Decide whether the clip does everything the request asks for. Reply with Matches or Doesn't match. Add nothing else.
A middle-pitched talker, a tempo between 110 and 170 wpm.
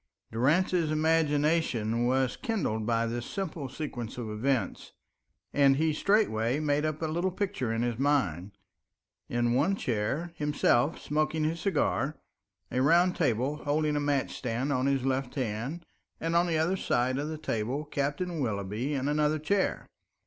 Matches